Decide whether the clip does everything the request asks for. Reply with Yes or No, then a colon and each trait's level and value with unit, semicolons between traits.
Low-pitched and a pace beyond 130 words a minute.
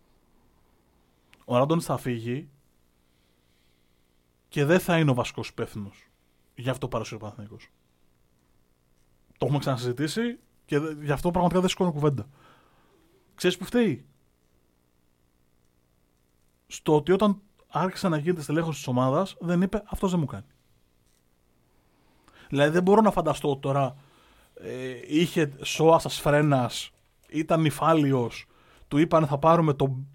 No: low, 130 Hz; average, 125 wpm